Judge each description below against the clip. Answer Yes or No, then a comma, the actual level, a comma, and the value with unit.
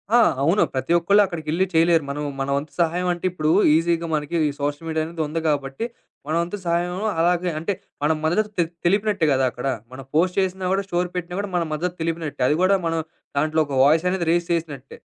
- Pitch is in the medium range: Yes, medium, 165 Hz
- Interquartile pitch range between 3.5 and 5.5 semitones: No, average, 2.7 semitones